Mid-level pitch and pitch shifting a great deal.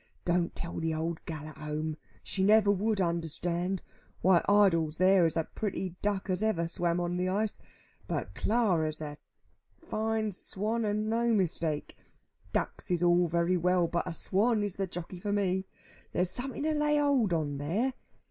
No: medium, 180 Hz; average, 3.7 semitones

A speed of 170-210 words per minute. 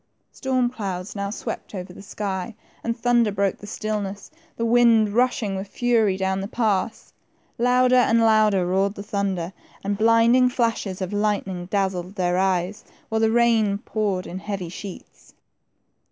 No: average, 155 wpm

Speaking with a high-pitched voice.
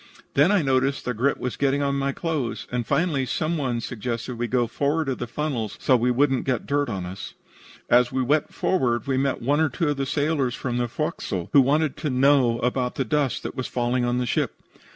No: low, 130 Hz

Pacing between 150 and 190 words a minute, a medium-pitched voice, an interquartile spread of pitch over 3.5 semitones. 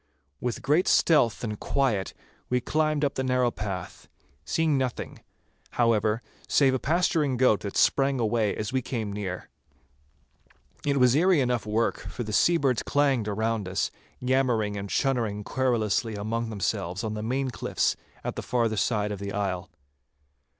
No: average, 155 wpm; low, 115 Hz; average, 4.1 semitones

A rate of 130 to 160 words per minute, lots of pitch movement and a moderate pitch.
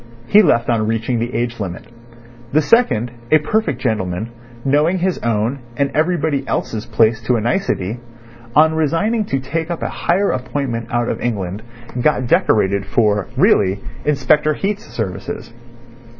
No: average, 150 wpm; wide, 6.1 semitones; low, 125 Hz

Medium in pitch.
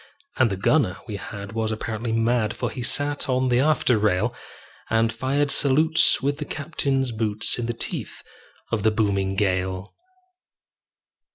No: low, 115 Hz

